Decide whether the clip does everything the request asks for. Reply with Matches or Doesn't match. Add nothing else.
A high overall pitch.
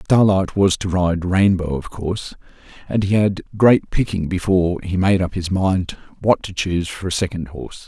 Doesn't match